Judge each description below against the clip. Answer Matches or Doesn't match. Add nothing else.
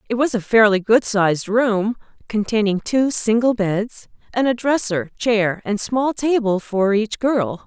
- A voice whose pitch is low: Doesn't match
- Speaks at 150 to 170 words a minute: Matches